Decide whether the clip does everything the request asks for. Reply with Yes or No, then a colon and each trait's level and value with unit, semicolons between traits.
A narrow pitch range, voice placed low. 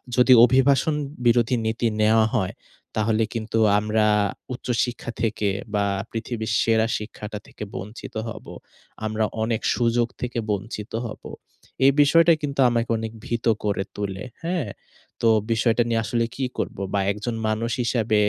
Yes: narrow, 2.0 semitones; low, 115 Hz